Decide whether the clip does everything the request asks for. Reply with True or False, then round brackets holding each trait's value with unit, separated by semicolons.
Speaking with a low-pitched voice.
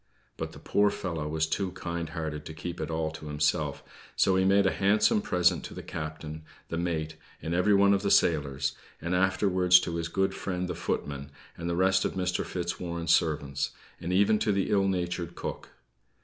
True (85 Hz)